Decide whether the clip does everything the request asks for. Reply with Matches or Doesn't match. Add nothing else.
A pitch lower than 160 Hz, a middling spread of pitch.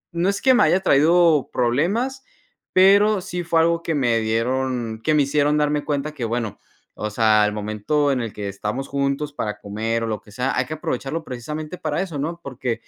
Doesn't match